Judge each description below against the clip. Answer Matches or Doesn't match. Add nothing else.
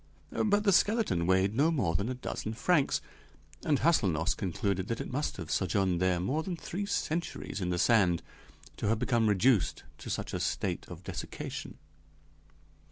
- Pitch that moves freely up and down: Matches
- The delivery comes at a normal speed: Matches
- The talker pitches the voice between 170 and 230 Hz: Doesn't match